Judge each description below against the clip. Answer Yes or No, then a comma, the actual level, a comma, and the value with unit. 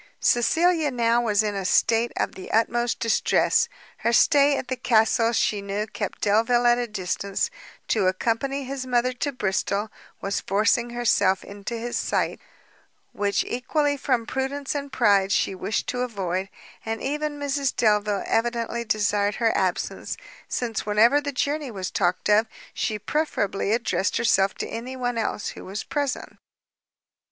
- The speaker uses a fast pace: No, average, 155 wpm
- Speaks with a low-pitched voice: No, high, 230 Hz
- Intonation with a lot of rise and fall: No, average, 3.8 semitones